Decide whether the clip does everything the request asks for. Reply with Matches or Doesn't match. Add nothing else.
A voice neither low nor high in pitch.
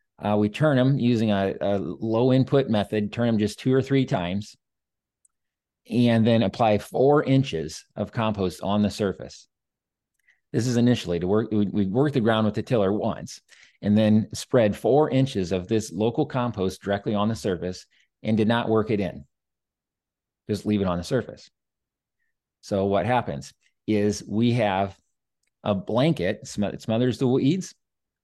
Doesn't match